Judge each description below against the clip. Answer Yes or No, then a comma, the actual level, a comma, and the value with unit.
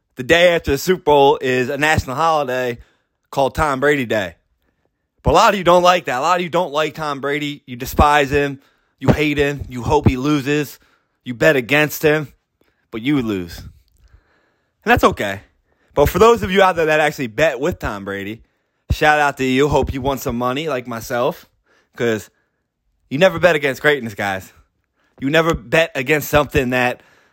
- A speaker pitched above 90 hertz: Yes, medium, 140 Hz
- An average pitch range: Yes, average, 3.8 semitones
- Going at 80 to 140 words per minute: No, average, 190 wpm